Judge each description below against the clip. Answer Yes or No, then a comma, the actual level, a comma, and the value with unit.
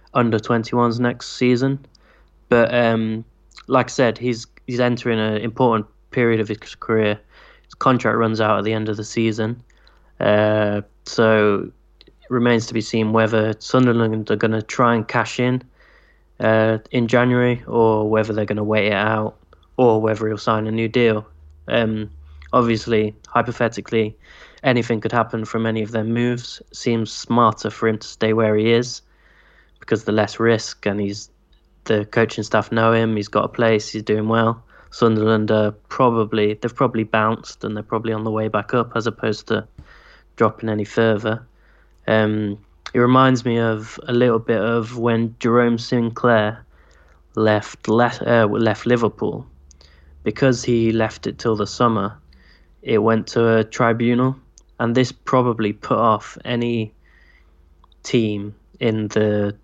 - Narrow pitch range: Yes, narrow, 1.8 semitones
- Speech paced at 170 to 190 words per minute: No, average, 160 wpm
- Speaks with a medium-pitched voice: No, low, 110 Hz